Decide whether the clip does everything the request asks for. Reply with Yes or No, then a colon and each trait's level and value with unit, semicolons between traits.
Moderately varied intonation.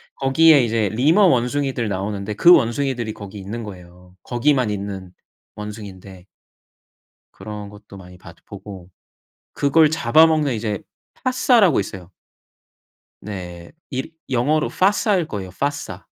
No: wide, 6.5 semitones